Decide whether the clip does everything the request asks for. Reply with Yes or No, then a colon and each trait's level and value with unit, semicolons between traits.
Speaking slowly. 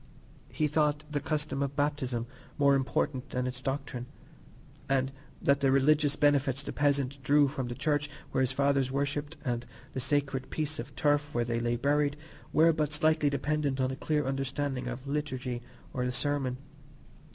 No: average, 175 wpm